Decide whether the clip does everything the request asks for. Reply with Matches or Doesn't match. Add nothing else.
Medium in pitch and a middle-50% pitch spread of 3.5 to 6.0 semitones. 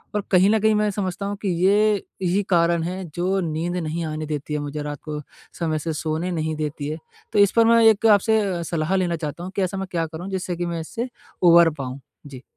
Matches